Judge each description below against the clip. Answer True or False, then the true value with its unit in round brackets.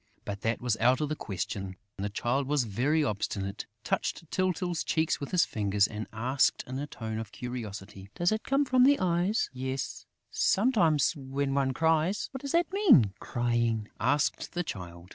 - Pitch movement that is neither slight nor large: False (7.6 semitones)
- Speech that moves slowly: False (175 wpm)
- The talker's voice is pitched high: False (135 Hz)